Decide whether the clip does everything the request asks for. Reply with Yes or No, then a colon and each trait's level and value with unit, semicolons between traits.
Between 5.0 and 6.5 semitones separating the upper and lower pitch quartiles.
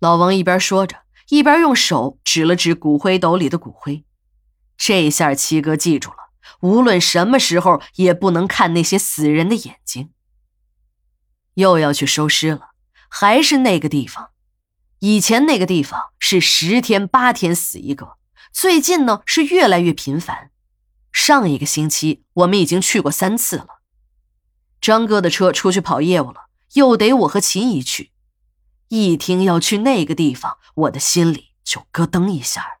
Yes: average, 5.3 semitones